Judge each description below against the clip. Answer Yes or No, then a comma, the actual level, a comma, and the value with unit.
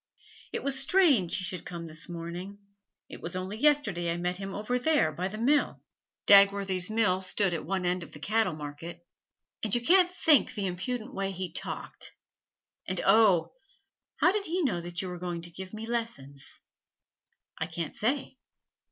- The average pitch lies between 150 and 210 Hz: Yes, high, 190 Hz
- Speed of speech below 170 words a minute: No, average, 180 wpm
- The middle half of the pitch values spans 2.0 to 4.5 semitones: No, average, 5.0 semitones